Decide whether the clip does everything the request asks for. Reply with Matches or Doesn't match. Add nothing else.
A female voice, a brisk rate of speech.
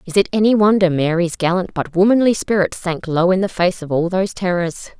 Matches